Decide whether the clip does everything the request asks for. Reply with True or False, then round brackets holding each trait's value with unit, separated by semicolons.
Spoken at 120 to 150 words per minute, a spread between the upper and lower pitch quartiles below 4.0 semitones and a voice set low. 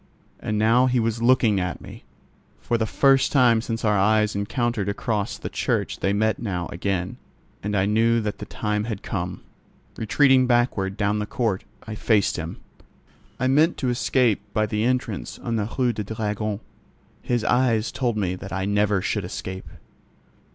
False (170 wpm; 2.8 semitones; 110 Hz)